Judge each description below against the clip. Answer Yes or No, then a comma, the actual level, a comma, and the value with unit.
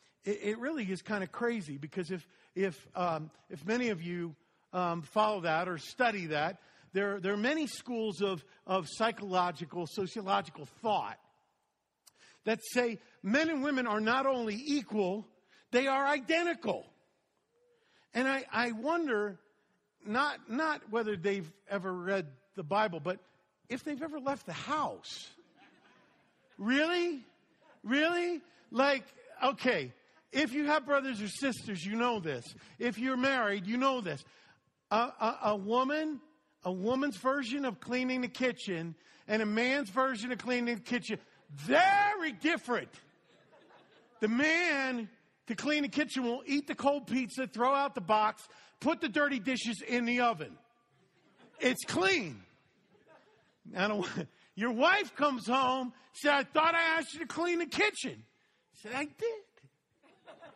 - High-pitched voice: Yes, high, 240 Hz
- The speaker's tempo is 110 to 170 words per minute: Yes, average, 145 wpm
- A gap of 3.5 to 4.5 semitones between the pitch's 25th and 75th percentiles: No, wide, 5.6 semitones